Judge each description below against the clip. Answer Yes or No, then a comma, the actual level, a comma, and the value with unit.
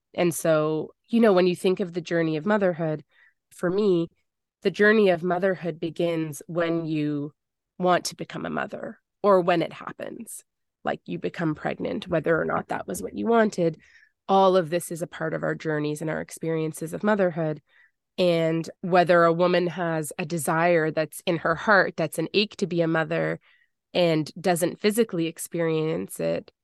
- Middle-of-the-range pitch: Yes, medium, 170 Hz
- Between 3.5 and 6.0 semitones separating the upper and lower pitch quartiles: No, narrow, 2.4 semitones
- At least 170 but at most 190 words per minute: Yes, average, 180 wpm